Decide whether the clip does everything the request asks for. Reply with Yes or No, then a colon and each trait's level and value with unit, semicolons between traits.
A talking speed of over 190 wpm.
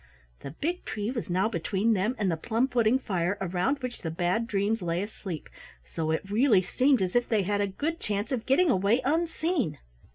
Yes: average, 200 wpm